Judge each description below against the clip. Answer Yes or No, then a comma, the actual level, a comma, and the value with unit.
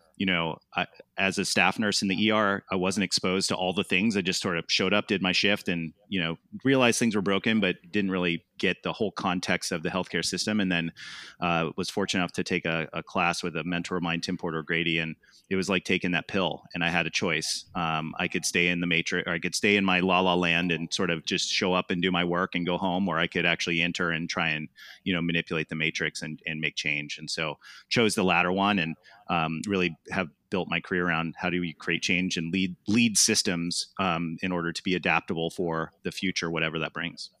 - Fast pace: Yes, fast, 250 wpm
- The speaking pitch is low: Yes, very low, 90 Hz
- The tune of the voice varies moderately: No, narrow, 2.2 semitones